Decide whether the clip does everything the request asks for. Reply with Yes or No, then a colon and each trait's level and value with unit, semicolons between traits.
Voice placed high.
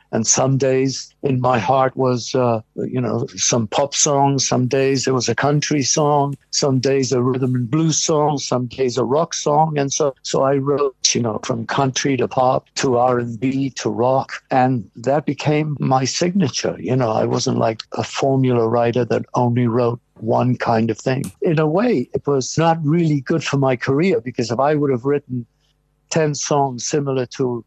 No: low, 135 Hz